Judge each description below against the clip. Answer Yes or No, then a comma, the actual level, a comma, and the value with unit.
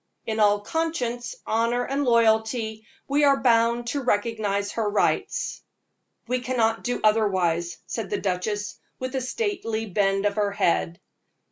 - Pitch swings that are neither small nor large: Yes, average, 3.3 semitones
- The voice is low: No, high, 225 Hz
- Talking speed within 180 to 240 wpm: No, average, 140 wpm